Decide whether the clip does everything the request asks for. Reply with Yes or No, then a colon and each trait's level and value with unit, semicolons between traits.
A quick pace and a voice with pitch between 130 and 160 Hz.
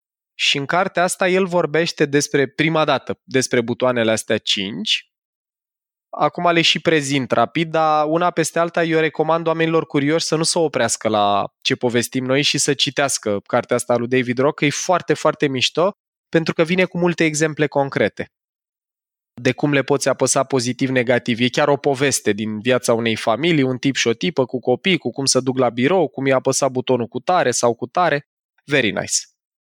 Yes: fast, 185 wpm; medium, 140 Hz